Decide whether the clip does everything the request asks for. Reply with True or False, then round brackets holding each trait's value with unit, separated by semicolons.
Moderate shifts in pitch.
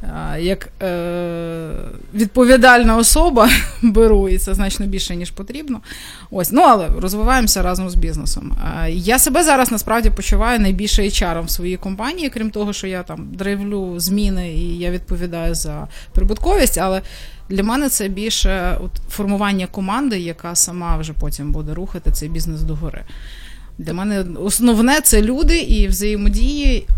True (4.3 semitones)